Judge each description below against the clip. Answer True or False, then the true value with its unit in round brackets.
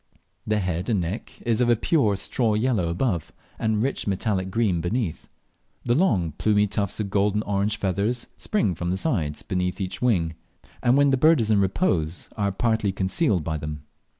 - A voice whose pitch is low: True (100 Hz)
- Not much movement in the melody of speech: False (4.2 semitones)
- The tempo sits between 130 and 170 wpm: False (180 wpm)